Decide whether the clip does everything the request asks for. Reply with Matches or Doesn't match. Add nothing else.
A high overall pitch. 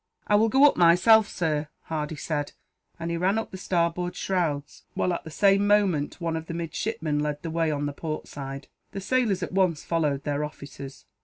Doesn't match